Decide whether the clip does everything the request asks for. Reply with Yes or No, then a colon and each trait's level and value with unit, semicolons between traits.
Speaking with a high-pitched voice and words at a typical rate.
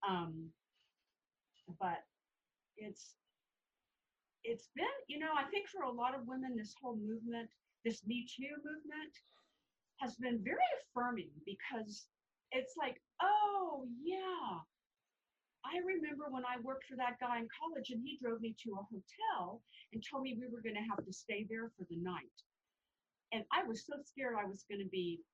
Yes: high, 245 Hz; average, 170 wpm